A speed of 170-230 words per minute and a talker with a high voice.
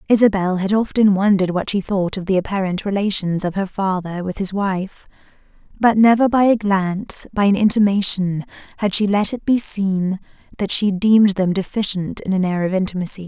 Yes: average, 185 wpm; high, 195 Hz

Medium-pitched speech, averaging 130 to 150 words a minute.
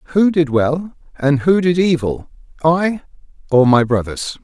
Yes: medium, 155 Hz; slow, 135 wpm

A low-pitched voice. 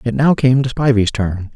Yes: low, 120 Hz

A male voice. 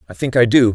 Yes: male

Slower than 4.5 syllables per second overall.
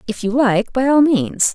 Yes: 4.3 syllables/s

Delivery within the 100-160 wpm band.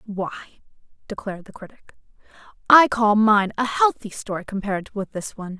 Yes: average, 150 wpm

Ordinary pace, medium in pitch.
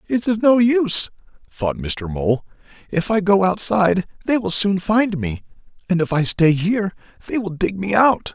Yes: average, 185 wpm; medium, 180 Hz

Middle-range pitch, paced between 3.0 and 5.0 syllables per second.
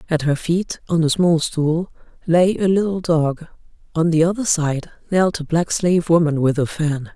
Yes: medium, 165 Hz; 4.6 syllables/s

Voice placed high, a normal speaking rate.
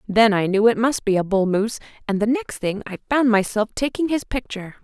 No: high, 225 Hz; fast, 235 wpm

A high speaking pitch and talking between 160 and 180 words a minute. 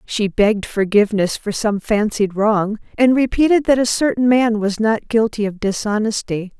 Yes: high, 220 Hz; average, 165 wpm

